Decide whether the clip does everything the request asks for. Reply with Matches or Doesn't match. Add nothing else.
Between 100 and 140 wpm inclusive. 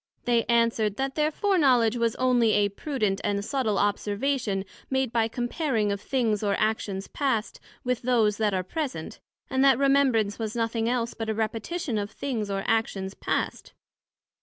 Doesn't match